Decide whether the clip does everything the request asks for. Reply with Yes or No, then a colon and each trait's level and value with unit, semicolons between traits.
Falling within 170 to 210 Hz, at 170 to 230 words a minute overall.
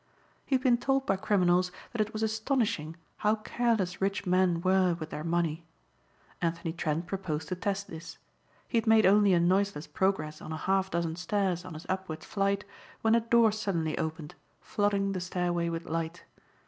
Yes: medium, 185 Hz; average, 180 wpm